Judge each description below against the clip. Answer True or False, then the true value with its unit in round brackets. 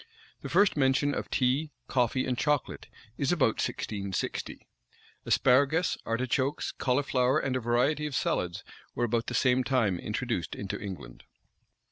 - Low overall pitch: True (125 Hz)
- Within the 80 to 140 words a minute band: True (135 wpm)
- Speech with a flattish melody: False (3.5 semitones)